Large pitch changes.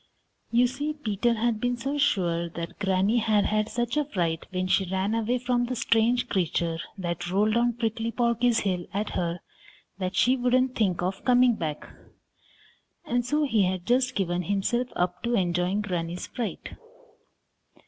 No: average, 4.9 semitones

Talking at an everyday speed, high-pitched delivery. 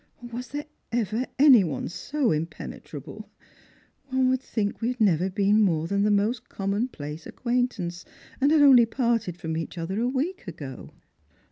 Yes: average, 155 wpm; high, 215 Hz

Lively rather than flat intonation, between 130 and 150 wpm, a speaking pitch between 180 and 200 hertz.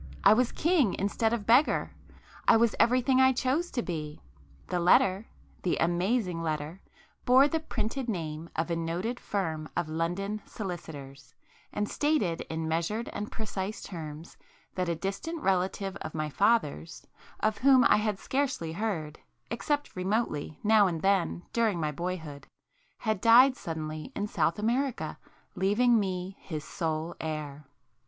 Yes: wide, 6.0 semitones; average, 140 wpm; high, 190 Hz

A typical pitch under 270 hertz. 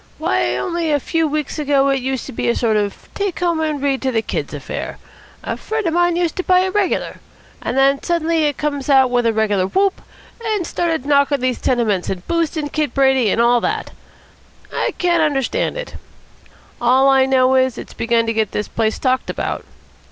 No: very high, 275 Hz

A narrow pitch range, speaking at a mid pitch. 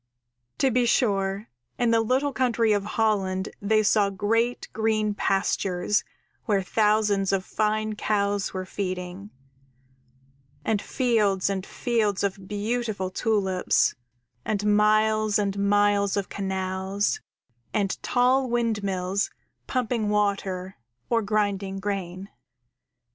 No: narrow, 2.1 semitones; high, 205 Hz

